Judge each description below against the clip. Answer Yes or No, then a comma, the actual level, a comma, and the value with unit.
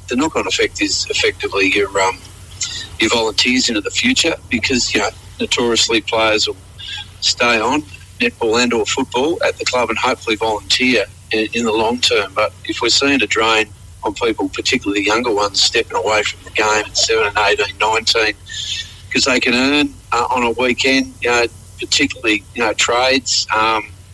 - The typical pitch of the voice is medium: No, low, 110 Hz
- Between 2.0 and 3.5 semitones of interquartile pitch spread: No, average, 5.0 semitones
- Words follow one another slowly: No, average, 180 wpm